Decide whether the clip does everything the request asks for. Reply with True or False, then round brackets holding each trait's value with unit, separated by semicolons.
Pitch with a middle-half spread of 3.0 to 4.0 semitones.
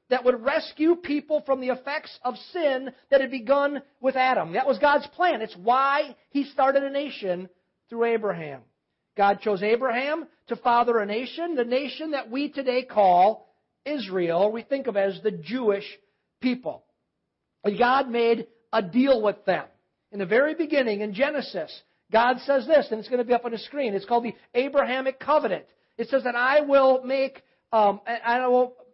True (3.7 semitones)